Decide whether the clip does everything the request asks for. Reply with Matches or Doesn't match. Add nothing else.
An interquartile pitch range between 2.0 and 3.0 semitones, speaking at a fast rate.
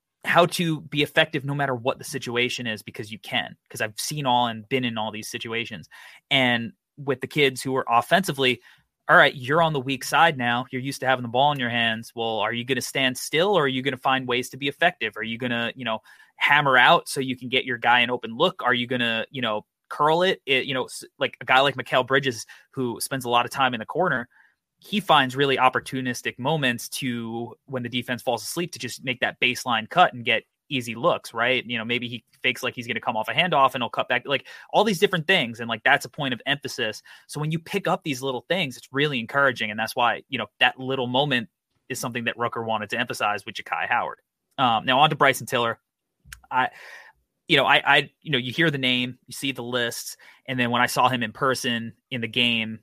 Matches